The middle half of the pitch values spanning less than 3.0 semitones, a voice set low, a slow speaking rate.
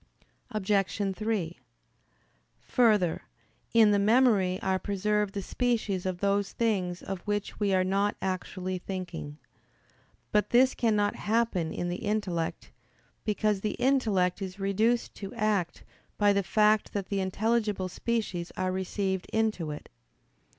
No: narrow, 2.5 semitones; high, 200 Hz; slow, 130 wpm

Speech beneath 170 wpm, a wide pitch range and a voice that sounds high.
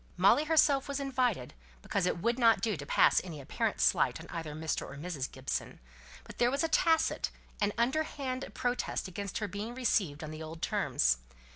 No: average, 185 wpm; wide, 8.3 semitones; high, 210 Hz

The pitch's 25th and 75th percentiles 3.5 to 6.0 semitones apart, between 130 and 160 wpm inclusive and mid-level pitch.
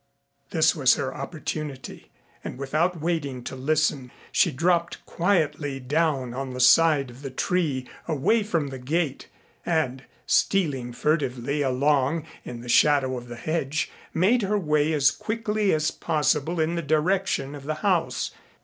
Yes: average, 3.9 semitones; average, 150 wpm; medium, 150 Hz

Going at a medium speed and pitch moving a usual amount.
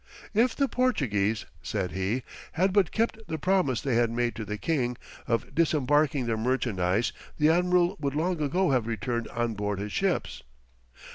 No: average, 165 wpm; wide, 7.4 semitones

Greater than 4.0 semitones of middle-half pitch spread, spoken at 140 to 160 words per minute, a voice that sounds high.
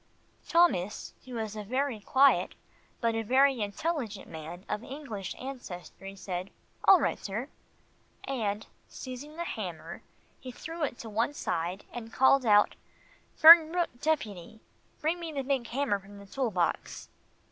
Yes: wide, 5.6 semitones; average, 145 wpm; high, 240 Hz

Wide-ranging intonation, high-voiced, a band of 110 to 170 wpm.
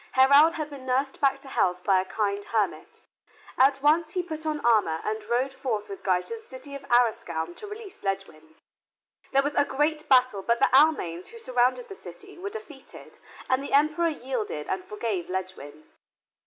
No: wide, 7.0 semitones; very high, 260 Hz; average, 185 wpm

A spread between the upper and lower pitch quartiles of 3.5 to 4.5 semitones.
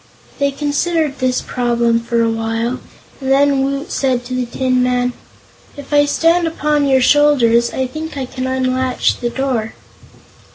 No: narrow, 2.6 semitones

